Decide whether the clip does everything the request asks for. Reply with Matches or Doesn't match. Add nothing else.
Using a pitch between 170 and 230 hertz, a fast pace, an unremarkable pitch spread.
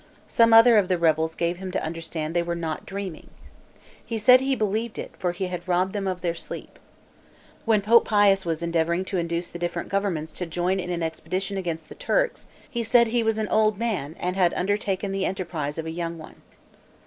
Matches